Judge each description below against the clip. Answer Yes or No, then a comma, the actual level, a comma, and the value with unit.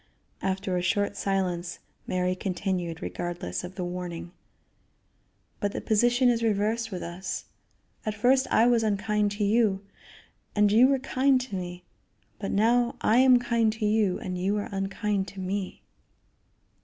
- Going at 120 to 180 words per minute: Yes, average, 155 wpm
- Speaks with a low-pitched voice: No, high, 205 Hz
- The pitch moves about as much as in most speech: Yes, average, 3.6 semitones